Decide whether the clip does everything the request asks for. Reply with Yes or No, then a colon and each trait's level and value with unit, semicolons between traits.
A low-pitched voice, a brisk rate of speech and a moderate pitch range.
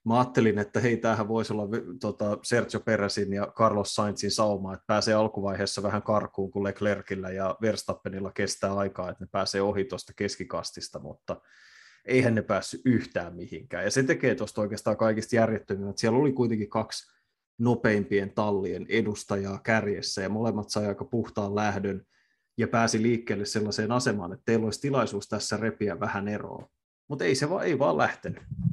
No: low, 105 Hz; fast, 165 wpm; narrow, 2.0 semitones